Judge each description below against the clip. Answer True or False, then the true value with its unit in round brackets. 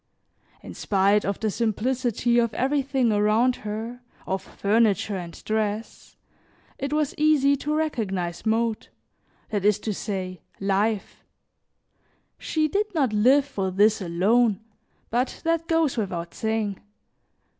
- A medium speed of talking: False (125 wpm)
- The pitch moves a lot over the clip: False (4.6 semitones)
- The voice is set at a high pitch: True (220 Hz)